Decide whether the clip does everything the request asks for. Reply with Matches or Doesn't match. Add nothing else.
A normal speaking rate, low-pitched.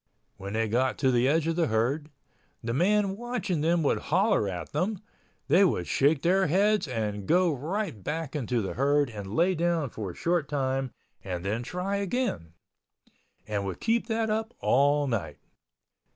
Doesn't match